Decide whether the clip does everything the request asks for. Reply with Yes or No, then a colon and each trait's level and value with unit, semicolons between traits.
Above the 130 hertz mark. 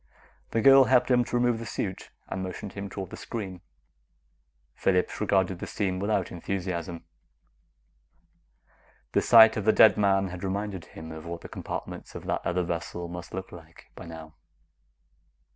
No: very low, 95 Hz